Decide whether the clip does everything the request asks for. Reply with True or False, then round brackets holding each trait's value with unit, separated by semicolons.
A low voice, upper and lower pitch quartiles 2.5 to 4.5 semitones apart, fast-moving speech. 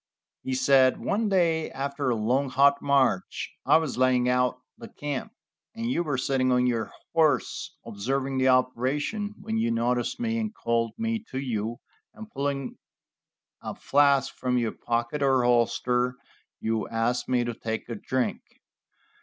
False (130 Hz; 2.8 semitones; 155 wpm)